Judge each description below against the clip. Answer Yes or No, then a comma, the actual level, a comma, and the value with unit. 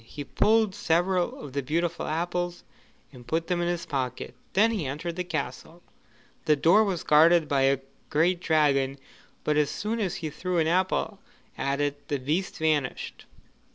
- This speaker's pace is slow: No, average, 170 wpm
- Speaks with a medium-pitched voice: Yes, medium, 160 Hz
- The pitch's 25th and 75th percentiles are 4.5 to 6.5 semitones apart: No, average, 3.7 semitones